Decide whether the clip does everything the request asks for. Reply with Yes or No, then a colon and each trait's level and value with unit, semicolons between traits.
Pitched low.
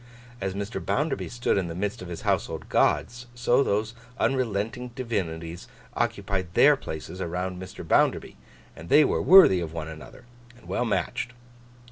Yes: low, 100 Hz